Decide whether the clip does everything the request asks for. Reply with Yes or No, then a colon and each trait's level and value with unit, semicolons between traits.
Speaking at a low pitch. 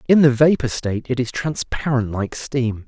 Yes: low, 130 Hz